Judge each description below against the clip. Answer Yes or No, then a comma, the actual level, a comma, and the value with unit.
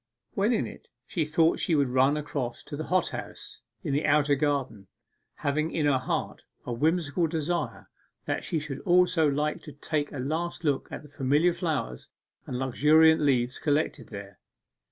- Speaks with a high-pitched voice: No, medium, 150 Hz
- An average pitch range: Yes, average, 3.0 semitones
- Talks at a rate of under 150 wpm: No, average, 175 wpm